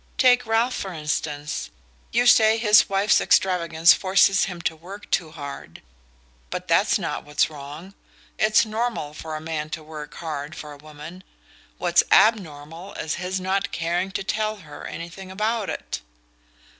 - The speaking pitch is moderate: Yes, medium, 180 Hz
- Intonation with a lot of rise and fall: No, average, 4.9 semitones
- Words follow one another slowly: No, average, 155 wpm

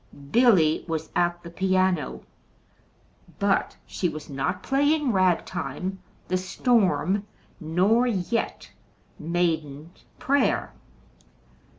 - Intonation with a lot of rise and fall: No, average, 4.3 semitones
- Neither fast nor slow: No, slow, 95 wpm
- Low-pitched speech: No, medium, 185 Hz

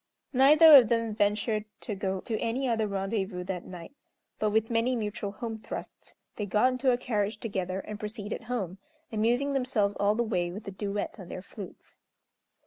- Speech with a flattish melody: No, average, 3.0 semitones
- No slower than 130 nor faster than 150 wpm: No, average, 180 wpm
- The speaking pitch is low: No, high, 215 Hz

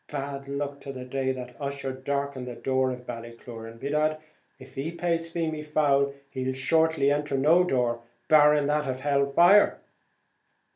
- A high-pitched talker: No, medium, 140 Hz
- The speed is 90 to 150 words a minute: No, average, 160 wpm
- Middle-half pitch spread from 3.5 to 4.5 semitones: No, narrow, 2.5 semitones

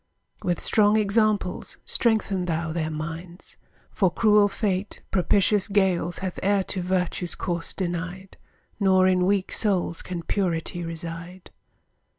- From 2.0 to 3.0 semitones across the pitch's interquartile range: Yes, narrow, 2.6 semitones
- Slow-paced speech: Yes, slow, 125 wpm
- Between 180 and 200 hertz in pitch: Yes, medium, 185 Hz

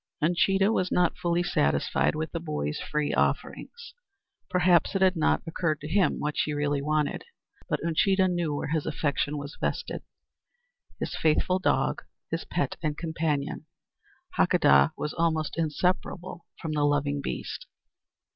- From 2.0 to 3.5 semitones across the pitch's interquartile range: Yes, average, 3.1 semitones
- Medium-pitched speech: Yes, medium, 160 Hz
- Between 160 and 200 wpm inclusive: No, average, 145 wpm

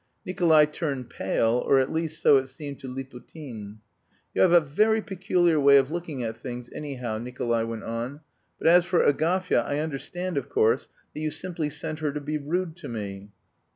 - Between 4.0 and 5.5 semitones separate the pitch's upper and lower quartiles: Yes, average, 5.2 semitones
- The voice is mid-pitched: Yes, medium, 145 Hz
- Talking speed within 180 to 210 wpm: Yes, average, 190 wpm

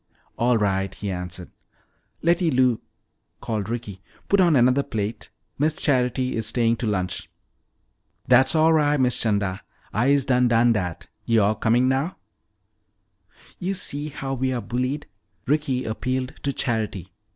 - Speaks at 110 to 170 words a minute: Yes, average, 140 wpm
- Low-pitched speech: Yes, low, 125 Hz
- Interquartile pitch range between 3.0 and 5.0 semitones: Yes, average, 4.1 semitones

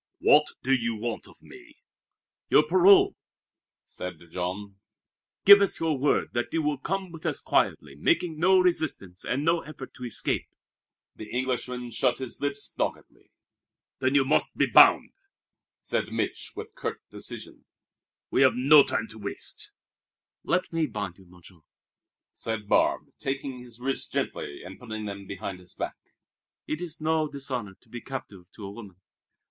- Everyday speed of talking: Yes, average, 155 wpm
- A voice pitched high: No, low, 130 Hz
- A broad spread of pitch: Yes, wide, 6.8 semitones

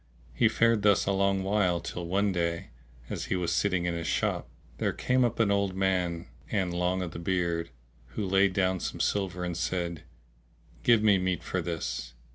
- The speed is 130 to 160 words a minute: No, average, 190 wpm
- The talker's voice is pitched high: No, very low, 95 Hz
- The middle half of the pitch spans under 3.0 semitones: Yes, narrow, 2.4 semitones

